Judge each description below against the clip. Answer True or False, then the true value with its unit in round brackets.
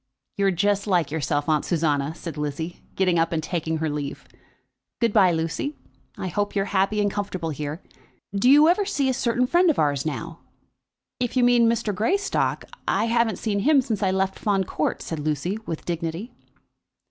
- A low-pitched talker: False (190 Hz)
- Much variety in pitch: True (6.0 semitones)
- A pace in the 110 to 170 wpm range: False (180 wpm)